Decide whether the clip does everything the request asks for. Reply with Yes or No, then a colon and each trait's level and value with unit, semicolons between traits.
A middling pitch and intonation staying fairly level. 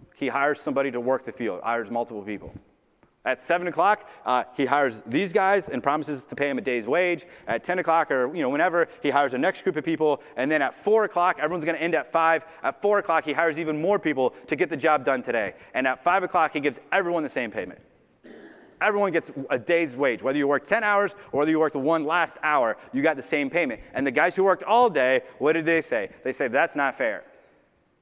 No: medium, 160 Hz; average, 4.5 semitones